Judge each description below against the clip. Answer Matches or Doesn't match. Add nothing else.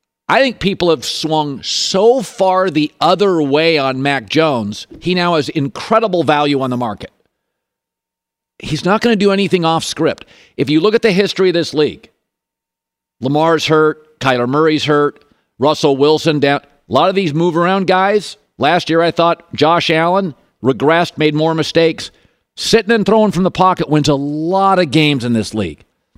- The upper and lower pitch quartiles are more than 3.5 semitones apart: Matches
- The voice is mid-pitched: Matches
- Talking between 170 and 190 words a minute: Matches